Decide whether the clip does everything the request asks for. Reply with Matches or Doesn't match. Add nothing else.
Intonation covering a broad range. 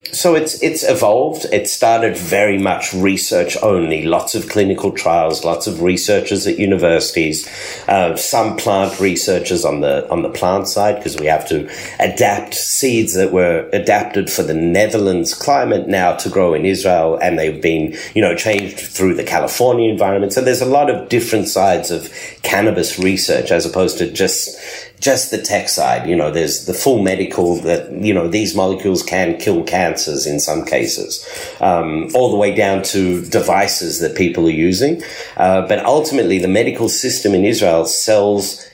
Matches